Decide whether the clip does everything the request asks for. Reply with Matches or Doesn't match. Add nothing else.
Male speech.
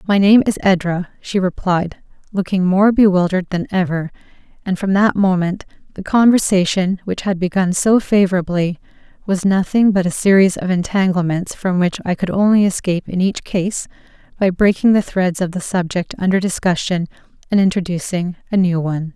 Doesn't match